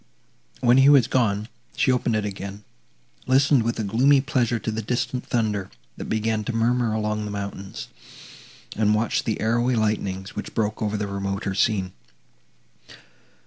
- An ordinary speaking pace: Yes, average, 155 wpm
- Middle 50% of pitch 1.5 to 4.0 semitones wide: Yes, average, 2.8 semitones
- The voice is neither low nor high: No, low, 110 Hz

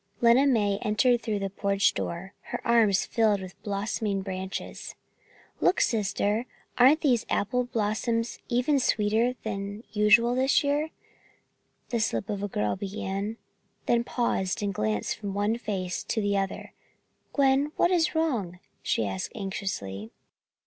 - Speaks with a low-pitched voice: No, high, 210 Hz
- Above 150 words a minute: No, slow, 135 wpm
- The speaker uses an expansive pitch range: No, average, 3.4 semitones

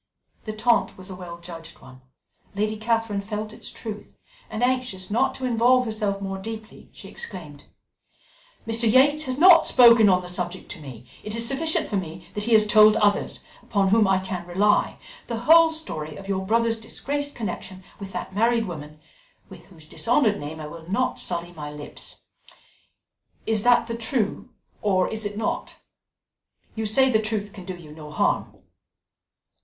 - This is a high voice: Yes, high, 210 Hz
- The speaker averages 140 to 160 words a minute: No, average, 175 wpm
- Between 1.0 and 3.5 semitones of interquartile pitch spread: No, average, 4.2 semitones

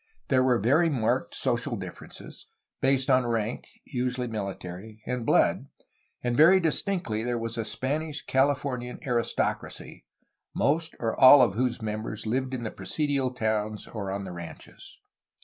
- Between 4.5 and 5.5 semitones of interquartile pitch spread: No, average, 3.5 semitones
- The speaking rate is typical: Yes, average, 145 wpm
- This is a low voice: Yes, low, 125 Hz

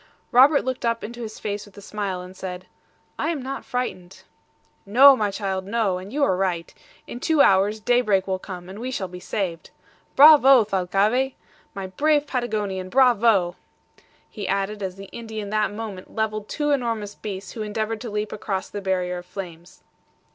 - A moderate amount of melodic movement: Yes, average, 4.1 semitones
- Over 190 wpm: No, average, 175 wpm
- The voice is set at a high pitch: Yes, high, 210 Hz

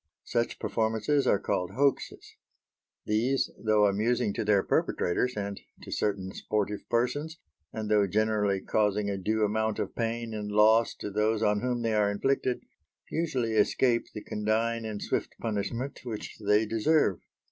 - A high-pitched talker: No, low, 110 Hz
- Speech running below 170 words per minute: Yes, average, 150 wpm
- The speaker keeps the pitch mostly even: Yes, narrow, 2.1 semitones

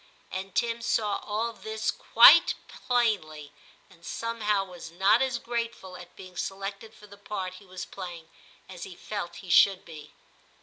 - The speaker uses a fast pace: No, average, 165 wpm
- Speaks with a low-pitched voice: No, high, 195 Hz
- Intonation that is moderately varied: Yes, average, 3.2 semitones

